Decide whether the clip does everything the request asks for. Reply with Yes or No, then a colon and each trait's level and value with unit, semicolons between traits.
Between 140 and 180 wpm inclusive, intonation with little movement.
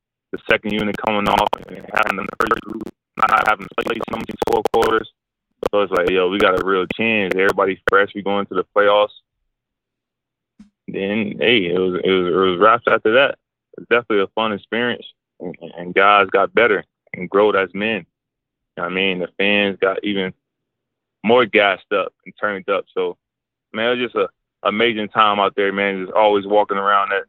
No: average, 195 wpm; narrow, 1.9 semitones